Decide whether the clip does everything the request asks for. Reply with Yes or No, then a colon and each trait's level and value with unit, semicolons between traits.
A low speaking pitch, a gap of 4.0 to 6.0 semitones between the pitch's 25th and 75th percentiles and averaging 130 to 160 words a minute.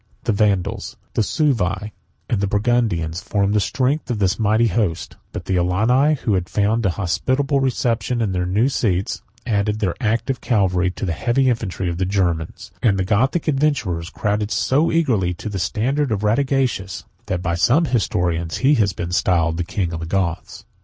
No: low, 105 Hz; average, 5.1 semitones; average, 180 wpm